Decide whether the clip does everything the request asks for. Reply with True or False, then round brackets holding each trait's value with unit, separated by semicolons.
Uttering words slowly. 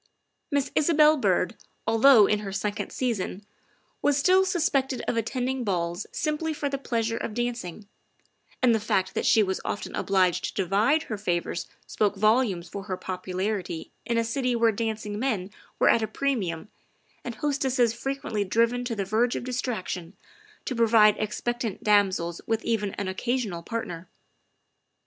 False (160 wpm)